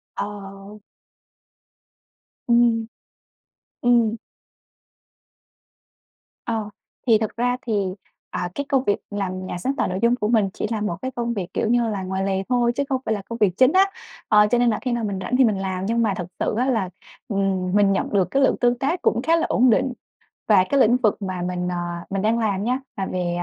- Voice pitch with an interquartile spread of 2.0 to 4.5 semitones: Yes, average, 3.8 semitones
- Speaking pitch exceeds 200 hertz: Yes, high, 215 Hz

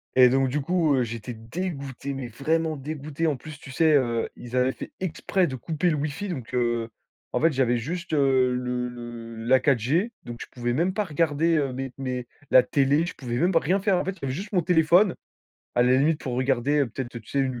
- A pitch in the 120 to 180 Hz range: Yes, low, 135 Hz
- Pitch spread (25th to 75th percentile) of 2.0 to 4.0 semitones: No, average, 4.5 semitones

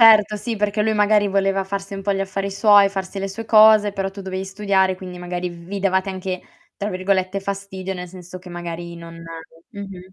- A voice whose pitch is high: Yes, high, 195 Hz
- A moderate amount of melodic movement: No, narrow, 1.5 semitones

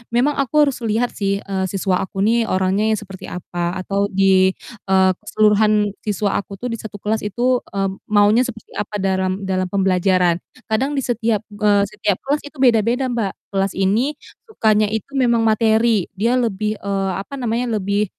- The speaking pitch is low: No, high, 210 Hz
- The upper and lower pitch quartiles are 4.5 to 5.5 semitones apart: No, average, 3.0 semitones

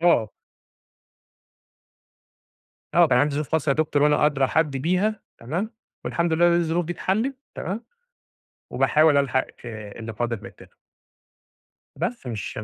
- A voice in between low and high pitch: Yes, medium, 150 Hz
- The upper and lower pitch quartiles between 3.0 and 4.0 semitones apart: No, average, 4.7 semitones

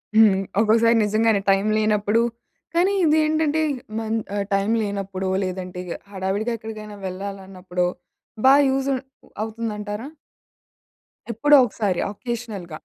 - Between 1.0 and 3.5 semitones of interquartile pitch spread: Yes, average, 2.9 semitones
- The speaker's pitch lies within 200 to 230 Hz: Yes, high, 215 Hz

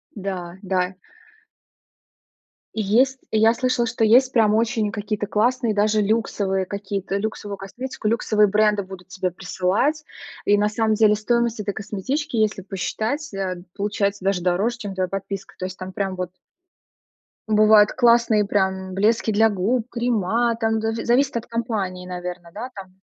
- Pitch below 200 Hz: No, high, 210 Hz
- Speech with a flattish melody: No, average, 3.0 semitones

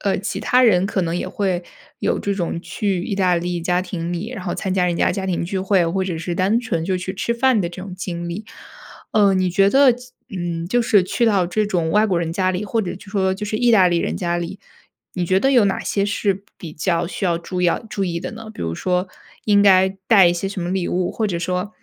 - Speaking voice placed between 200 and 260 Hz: No, medium, 185 Hz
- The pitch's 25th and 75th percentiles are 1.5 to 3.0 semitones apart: Yes, average, 2.7 semitones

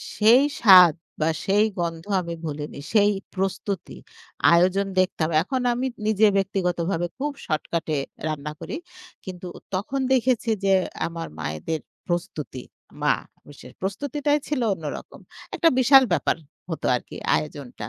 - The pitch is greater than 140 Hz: Yes, medium, 185 Hz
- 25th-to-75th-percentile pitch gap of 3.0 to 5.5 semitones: Yes, average, 5.1 semitones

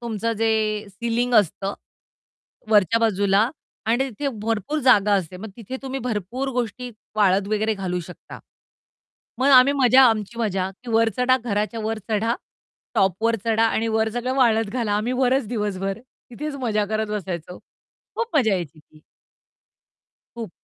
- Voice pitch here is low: No, high, 220 Hz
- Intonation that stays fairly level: No, average, 3.1 semitones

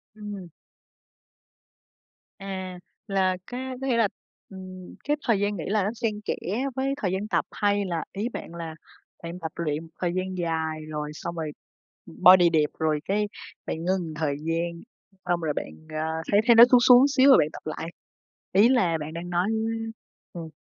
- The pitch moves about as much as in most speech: Yes, average, 4.2 semitones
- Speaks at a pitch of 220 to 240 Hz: No, medium, 185 Hz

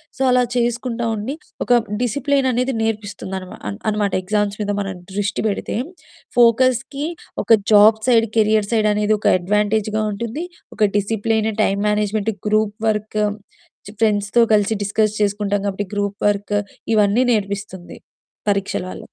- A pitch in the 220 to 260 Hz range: No, high, 210 Hz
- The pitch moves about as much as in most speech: No, narrow, 1.9 semitones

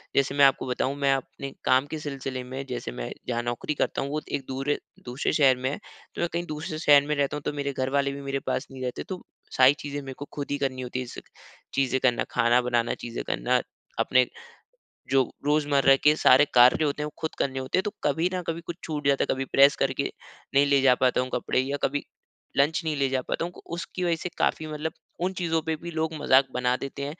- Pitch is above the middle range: No, medium, 140 Hz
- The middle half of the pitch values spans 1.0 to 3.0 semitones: Yes, narrow, 2.5 semitones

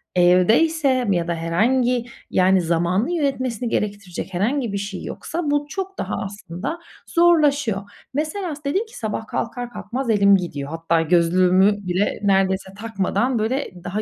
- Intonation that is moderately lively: No, wide, 7.2 semitones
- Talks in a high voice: Yes, high, 210 Hz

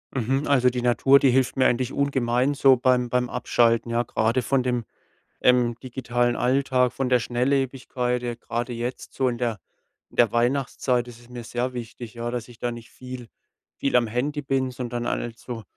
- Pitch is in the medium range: No, low, 125 Hz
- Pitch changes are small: Yes, narrow, 1.4 semitones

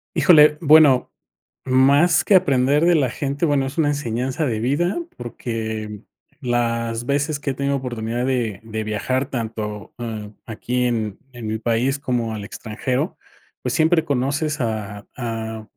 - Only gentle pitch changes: No, average, 4.0 semitones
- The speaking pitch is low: Yes, low, 125 Hz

